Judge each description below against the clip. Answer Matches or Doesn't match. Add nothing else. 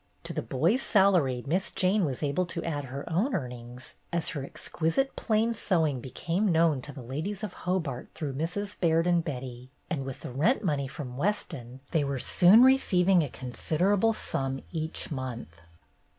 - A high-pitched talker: Doesn't match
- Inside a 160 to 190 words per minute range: Matches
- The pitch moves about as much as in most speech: Doesn't match